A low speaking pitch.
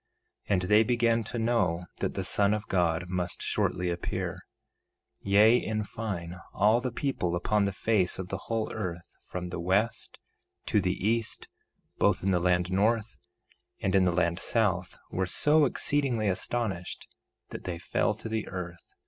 Yes: low, 100 Hz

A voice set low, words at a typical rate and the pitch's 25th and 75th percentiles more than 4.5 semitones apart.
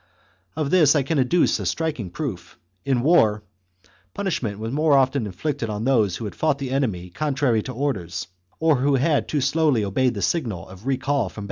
Yes: low, 130 Hz; average, 190 wpm; wide, 5.5 semitones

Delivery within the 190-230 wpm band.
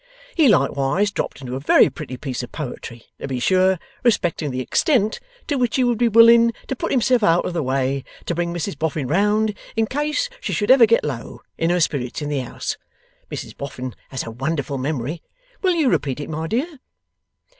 Yes: average, 200 wpm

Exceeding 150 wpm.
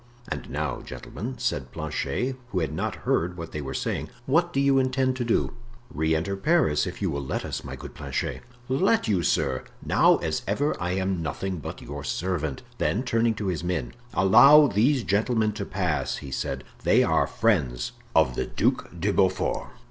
Yes: average, 185 wpm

